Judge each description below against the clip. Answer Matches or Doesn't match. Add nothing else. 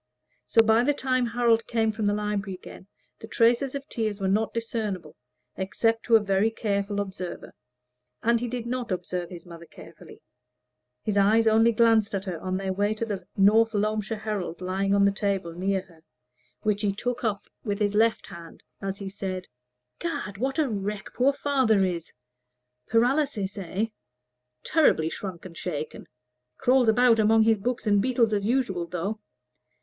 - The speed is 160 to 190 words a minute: Matches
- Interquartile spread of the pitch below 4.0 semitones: Matches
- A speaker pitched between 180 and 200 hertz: Doesn't match